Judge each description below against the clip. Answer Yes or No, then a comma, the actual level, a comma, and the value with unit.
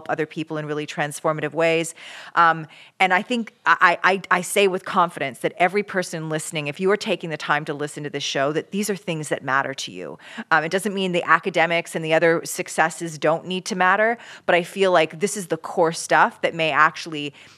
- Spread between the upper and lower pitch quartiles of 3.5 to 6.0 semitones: No, average, 3.0 semitones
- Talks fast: Yes, fast, 220 wpm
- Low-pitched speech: No, medium, 165 Hz